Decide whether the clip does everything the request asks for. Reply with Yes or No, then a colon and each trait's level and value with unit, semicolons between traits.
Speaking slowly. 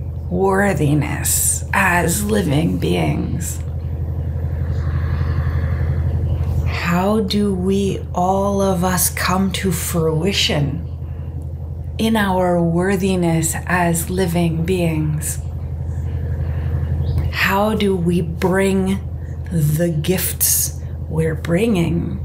Yes: slow, 75 wpm